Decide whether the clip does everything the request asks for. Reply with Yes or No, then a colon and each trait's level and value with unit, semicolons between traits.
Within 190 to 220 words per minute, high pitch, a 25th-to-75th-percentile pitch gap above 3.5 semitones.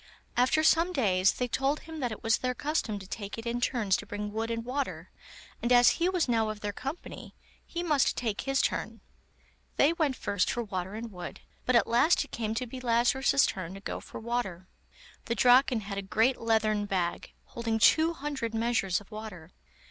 Yes: average, 200 wpm; high, 230 Hz; average, 4.2 semitones